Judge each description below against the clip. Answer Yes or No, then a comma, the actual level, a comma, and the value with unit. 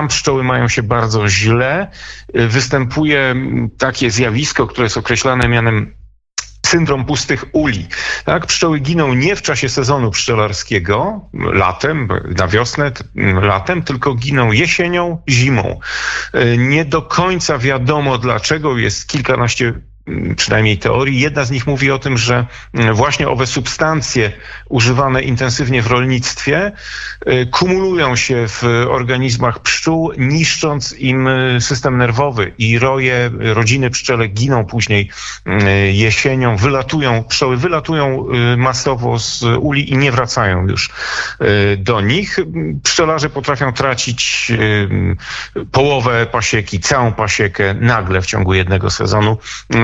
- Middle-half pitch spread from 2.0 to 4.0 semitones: Yes, average, 3.5 semitones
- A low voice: Yes, low, 125 Hz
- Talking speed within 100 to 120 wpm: Yes, average, 115 wpm